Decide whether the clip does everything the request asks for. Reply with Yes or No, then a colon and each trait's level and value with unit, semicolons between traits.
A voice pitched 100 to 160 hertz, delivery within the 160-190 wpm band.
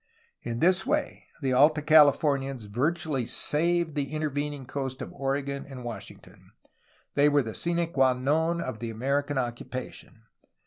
No: medium, 140 Hz; average, 150 wpm